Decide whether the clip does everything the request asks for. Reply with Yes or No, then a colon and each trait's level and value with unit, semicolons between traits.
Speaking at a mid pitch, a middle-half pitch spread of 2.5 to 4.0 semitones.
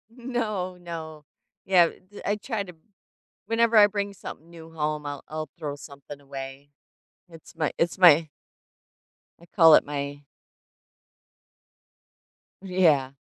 No: medium, 165 Hz; average, 4.7 semitones